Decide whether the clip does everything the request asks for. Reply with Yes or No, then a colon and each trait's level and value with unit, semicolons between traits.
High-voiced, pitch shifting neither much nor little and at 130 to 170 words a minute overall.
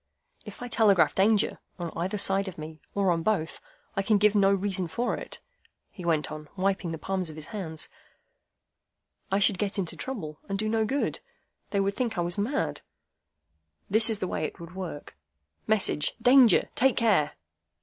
No: high, 195 Hz; average, 4.4 semitones; average, 180 wpm